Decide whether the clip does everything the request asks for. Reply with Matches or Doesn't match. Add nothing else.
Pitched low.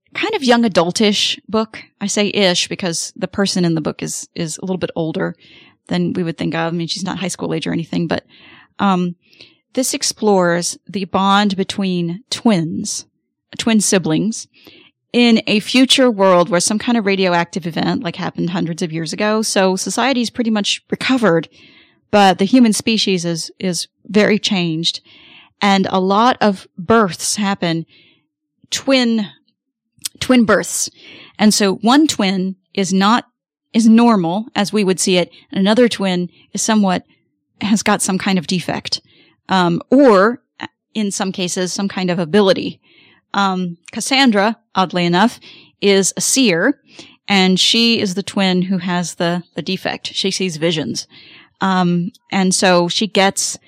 Doesn't match